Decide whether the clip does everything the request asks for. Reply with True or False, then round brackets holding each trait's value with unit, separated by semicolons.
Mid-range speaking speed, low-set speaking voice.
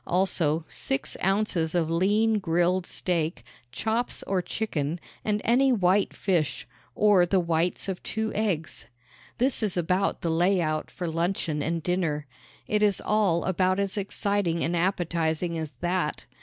False (145 wpm; 180 Hz)